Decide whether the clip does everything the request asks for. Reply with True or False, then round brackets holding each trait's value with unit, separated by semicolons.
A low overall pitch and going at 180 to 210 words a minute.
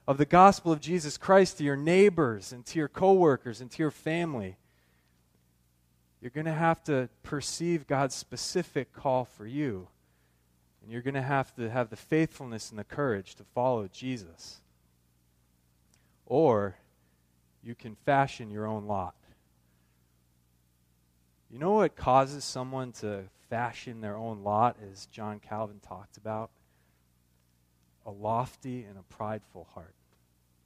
False (110 Hz; 140 wpm)